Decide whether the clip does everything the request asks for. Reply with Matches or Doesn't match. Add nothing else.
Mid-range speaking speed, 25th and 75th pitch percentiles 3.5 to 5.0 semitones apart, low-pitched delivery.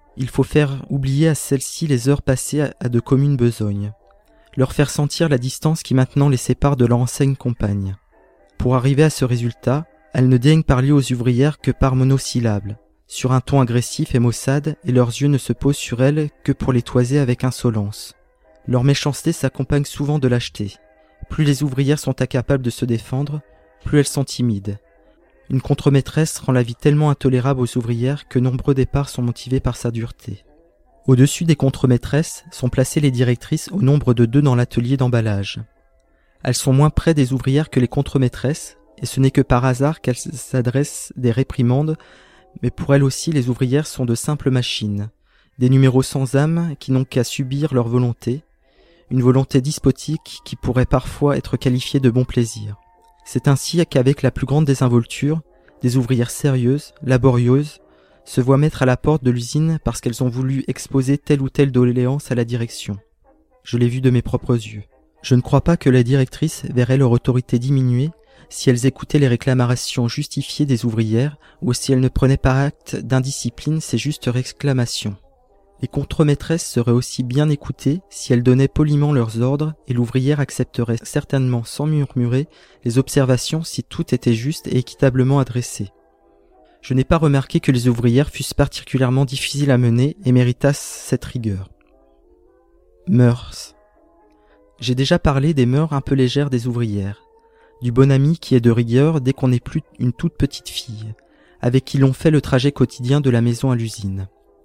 Doesn't match